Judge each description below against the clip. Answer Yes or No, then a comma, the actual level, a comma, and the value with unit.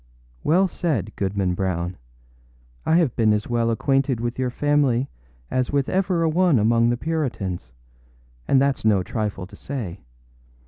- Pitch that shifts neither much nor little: No, wide, 5.9 semitones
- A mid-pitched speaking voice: No, low, 120 Hz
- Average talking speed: Yes, average, 150 wpm